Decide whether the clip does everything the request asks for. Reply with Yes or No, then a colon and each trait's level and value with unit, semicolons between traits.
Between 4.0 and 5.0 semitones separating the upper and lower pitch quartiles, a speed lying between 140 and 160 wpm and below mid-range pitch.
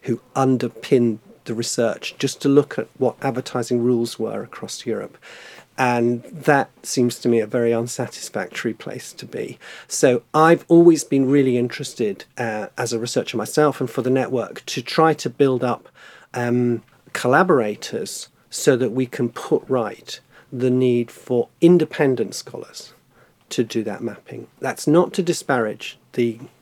No: average, 2.7 semitones; average, 150 wpm; low, 125 Hz